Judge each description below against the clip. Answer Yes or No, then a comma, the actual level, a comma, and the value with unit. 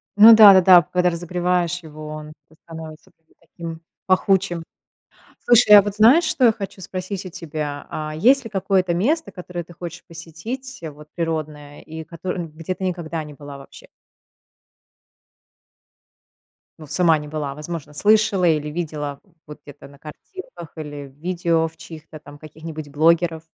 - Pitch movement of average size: Yes, average, 3.4 semitones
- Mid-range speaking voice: Yes, medium, 165 Hz